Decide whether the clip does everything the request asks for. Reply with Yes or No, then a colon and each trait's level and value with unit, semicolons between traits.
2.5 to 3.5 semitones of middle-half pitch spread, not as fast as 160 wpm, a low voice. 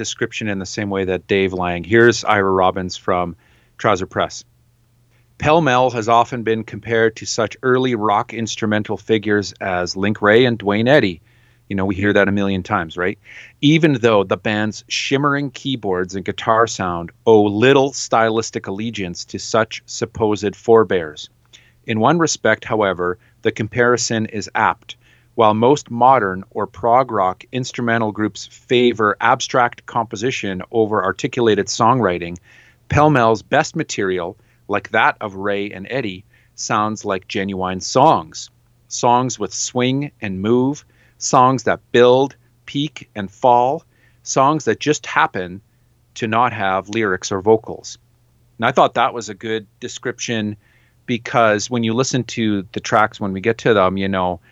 Yes: average, 3.2 semitones; average, 150 wpm; low, 115 Hz